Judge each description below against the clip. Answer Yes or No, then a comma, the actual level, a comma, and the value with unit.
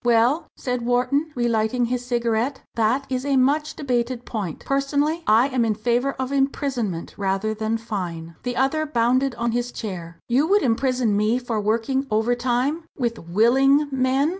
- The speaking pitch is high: Yes, high, 245 Hz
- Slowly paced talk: No, average, 160 wpm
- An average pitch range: Yes, average, 3.4 semitones